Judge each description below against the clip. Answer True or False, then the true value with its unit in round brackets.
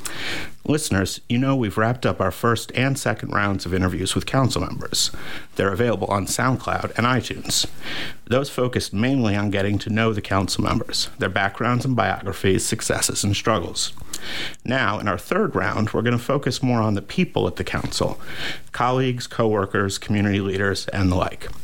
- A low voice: True (110 Hz)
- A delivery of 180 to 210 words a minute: False (170 wpm)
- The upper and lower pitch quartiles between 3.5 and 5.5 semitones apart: True (3.9 semitones)